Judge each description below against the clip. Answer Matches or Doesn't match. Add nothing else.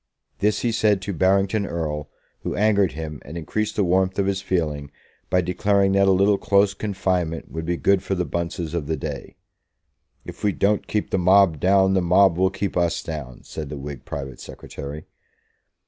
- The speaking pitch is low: Matches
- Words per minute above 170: Matches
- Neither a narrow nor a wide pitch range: Matches